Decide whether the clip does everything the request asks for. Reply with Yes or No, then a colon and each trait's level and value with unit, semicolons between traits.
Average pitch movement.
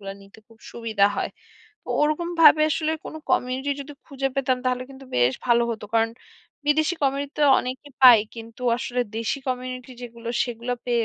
Yes: average, 3.3 semitones